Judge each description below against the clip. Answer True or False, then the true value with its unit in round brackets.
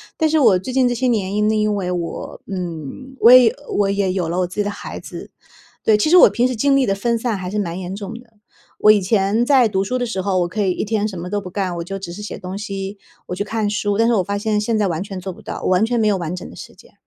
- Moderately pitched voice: False (205 Hz)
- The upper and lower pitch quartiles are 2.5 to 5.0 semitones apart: True (3.3 semitones)